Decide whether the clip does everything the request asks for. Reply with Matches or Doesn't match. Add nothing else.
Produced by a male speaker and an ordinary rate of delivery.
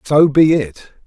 Matches